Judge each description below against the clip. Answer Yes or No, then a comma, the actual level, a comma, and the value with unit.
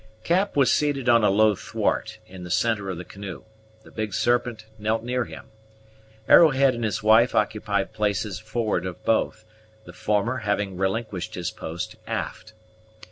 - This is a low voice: Yes, low, 110 Hz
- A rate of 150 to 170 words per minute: Yes, average, 160 wpm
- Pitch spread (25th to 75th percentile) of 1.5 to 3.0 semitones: No, average, 3.5 semitones